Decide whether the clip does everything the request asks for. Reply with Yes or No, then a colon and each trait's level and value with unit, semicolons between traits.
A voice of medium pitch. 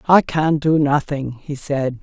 Yes: medium, 145 Hz